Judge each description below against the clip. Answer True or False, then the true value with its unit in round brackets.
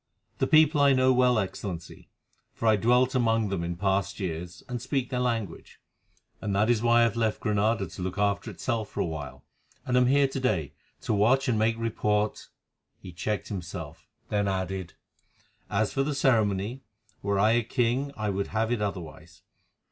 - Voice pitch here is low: True (110 Hz)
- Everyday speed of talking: True (185 wpm)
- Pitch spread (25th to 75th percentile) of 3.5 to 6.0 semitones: True (4.0 semitones)